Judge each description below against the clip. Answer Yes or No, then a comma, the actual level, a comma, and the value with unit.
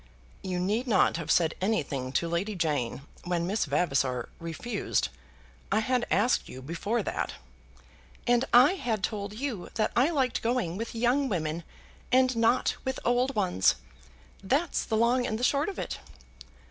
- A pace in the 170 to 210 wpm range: No, average, 160 wpm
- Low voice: No, high, 215 Hz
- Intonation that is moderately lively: No, wide, 6.5 semitones